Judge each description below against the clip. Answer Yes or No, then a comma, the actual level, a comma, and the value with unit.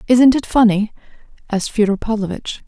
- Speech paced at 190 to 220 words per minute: No, slow, 135 wpm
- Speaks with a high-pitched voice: Yes, high, 220 Hz